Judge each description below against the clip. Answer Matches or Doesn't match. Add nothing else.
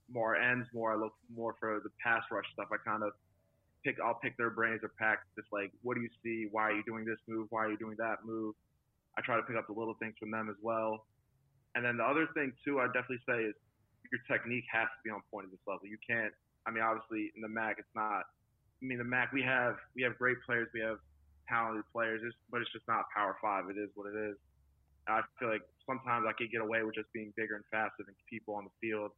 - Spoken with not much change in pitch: Matches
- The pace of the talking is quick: Matches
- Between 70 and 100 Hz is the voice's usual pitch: Doesn't match